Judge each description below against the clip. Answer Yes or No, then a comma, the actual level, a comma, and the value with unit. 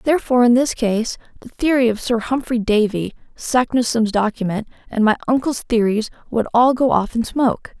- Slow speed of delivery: No, average, 170 wpm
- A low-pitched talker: No, high, 235 Hz